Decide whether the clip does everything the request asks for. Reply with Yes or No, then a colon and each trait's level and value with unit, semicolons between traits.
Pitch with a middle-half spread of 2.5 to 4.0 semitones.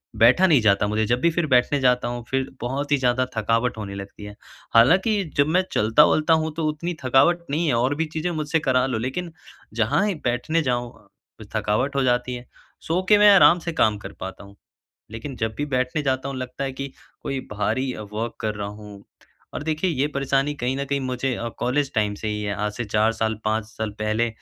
No: average, 5.0 semitones